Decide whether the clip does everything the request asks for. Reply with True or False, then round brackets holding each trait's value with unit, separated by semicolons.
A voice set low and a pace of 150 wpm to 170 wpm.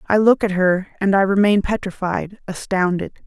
False (195 Hz; 165 wpm)